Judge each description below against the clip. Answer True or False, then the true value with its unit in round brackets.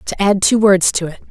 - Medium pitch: False (195 Hz)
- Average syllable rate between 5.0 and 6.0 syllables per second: True (5.3 syllables/s)